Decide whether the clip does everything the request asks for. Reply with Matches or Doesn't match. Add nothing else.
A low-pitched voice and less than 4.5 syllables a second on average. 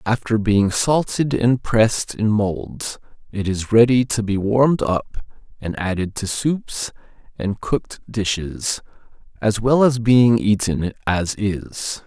Matches